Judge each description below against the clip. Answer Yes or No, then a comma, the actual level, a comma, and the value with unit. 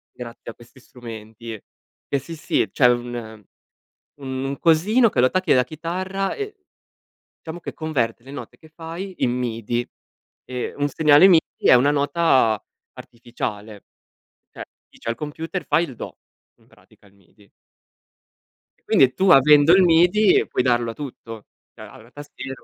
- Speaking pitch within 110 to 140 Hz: Yes, low, 135 Hz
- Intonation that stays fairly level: No, wide, 5.6 semitones